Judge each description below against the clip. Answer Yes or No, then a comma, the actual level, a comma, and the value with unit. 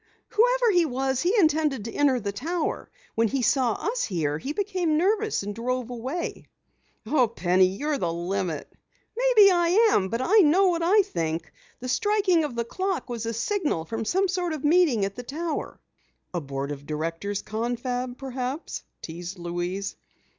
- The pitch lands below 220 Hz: No, very high, 255 Hz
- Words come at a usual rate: Yes, average, 170 wpm